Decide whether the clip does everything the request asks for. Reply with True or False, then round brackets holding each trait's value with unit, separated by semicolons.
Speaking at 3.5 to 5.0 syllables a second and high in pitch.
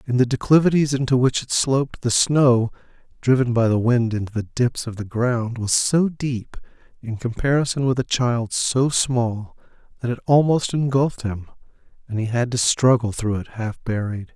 False (4.8 syllables/s; 120 Hz)